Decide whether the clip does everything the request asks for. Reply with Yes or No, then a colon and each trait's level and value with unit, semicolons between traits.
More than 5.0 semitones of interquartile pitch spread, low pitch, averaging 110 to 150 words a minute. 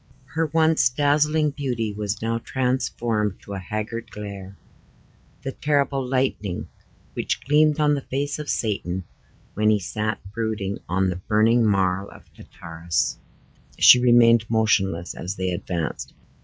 Yes: wide, 5.4 semitones; low, 110 Hz; slow, 135 wpm